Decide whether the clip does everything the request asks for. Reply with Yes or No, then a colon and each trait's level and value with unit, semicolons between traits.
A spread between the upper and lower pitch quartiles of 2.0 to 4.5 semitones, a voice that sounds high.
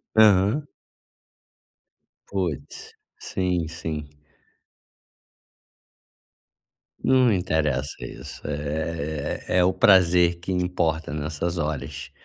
No: average, 3.4 semitones; very low, 85 Hz